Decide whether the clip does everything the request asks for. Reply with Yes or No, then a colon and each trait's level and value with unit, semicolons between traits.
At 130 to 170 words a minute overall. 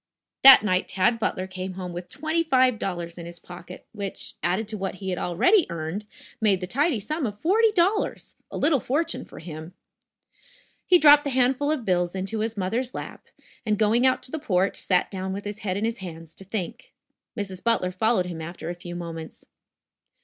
No: average, 200 wpm